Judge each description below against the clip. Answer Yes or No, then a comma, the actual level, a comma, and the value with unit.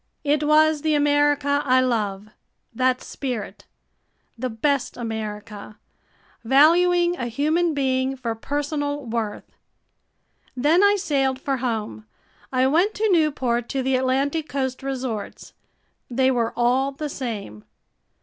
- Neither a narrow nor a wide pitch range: Yes, average, 3.6 semitones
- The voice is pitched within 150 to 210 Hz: No, very high, 265 Hz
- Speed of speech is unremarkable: No, slow, 120 wpm